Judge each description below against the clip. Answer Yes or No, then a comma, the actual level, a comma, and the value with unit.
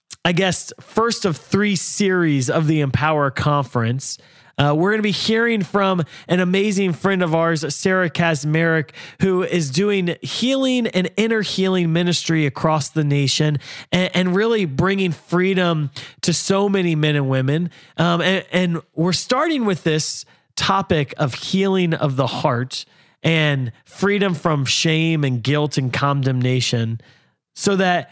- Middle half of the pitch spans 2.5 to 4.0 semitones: No, average, 4.4 semitones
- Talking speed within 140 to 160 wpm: Yes, average, 145 wpm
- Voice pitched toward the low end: No, medium, 165 Hz